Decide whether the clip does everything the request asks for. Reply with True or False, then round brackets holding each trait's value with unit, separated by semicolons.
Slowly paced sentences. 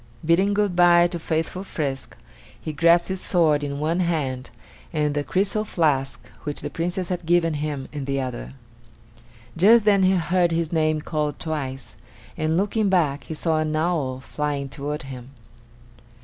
False (165 wpm)